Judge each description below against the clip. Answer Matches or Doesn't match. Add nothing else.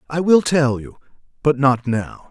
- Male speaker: Matches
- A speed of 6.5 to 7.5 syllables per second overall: Doesn't match